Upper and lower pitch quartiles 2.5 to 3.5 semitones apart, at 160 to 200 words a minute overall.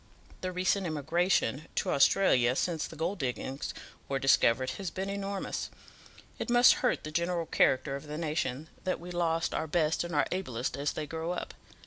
No: average, 4.5 semitones; average, 175 wpm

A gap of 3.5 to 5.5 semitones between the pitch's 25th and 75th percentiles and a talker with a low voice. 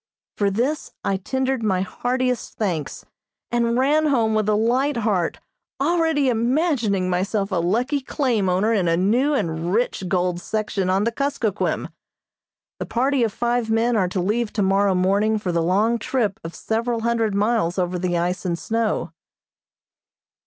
No: average, 4.5 semitones; high, 220 Hz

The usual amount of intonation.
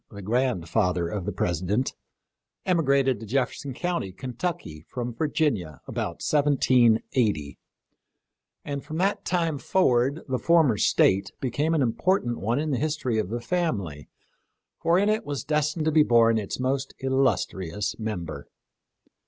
No: wide, 6.5 semitones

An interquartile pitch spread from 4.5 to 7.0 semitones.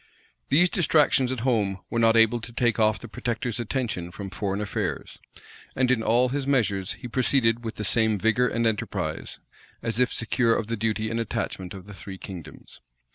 No: average, 2.9 semitones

